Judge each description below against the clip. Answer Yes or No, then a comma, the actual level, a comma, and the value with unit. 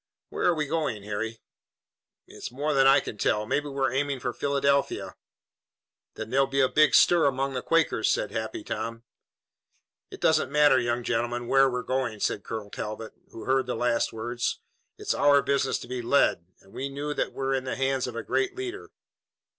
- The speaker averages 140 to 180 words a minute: No, average, 190 wpm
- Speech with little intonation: No, average, 3.3 semitones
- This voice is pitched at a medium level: No, low, 130 Hz